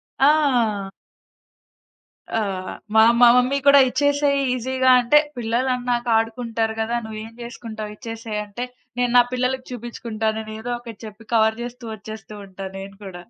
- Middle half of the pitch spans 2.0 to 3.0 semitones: Yes, narrow, 2.4 semitones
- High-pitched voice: Yes, high, 230 Hz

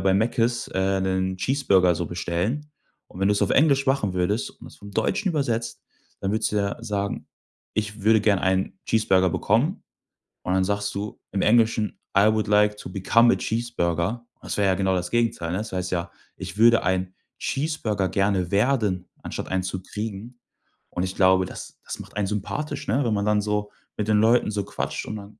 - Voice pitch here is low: Yes, low, 105 Hz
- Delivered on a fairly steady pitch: No, average, 3.2 semitones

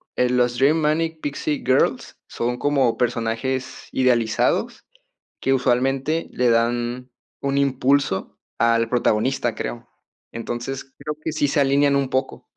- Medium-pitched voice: No, low, 130 Hz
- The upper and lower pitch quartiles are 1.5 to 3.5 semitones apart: Yes, average, 2.7 semitones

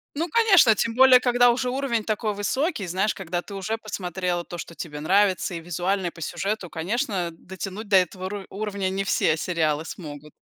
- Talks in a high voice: Yes, high, 195 Hz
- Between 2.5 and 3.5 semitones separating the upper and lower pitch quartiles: No, average, 4.1 semitones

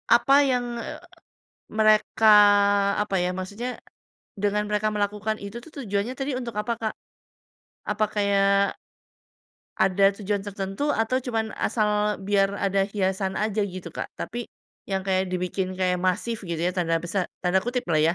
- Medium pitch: No, high, 200 Hz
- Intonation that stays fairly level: Yes, narrow, 2.3 semitones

